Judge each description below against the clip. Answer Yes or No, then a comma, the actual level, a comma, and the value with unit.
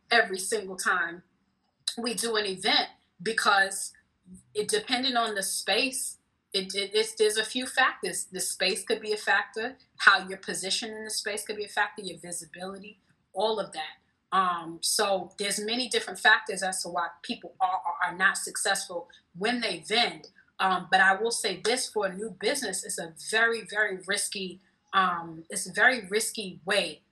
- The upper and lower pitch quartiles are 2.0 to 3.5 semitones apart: Yes, average, 3.0 semitones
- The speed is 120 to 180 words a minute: Yes, average, 175 wpm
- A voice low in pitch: No, high, 200 Hz